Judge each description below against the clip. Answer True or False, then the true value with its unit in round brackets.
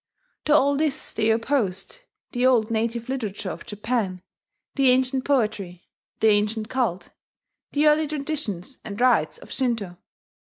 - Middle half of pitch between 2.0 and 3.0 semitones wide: False (4.5 semitones)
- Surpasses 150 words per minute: False (135 wpm)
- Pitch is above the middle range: True (235 Hz)